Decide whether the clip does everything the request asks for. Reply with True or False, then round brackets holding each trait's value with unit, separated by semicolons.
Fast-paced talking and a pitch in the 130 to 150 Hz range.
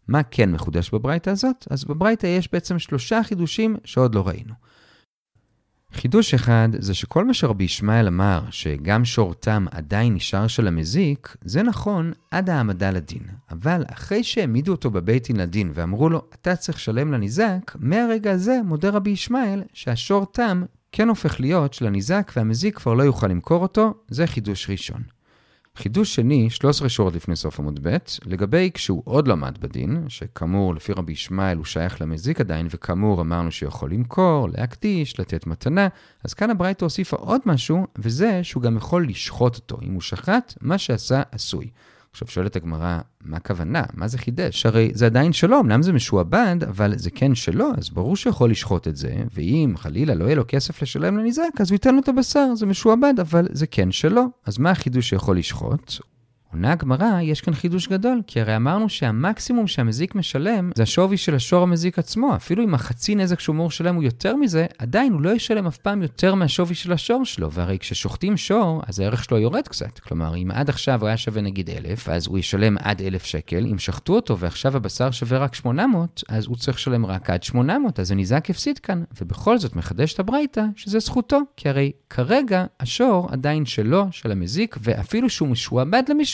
True (175 wpm; 135 Hz)